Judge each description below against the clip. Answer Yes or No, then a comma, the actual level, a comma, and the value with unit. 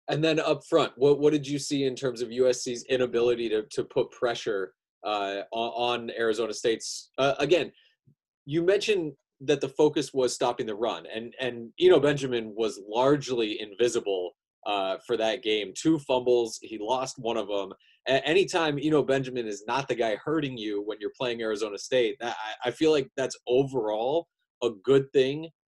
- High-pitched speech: No, low, 130 Hz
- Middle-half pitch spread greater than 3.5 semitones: Yes, average, 4.5 semitones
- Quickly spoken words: No, average, 185 wpm